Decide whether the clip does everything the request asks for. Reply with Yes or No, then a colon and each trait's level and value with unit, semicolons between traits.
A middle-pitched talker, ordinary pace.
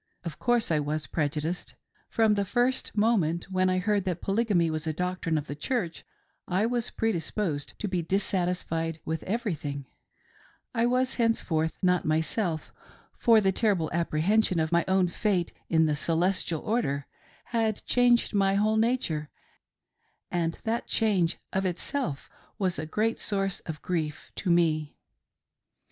Yes: medium, 180 Hz; average, 150 wpm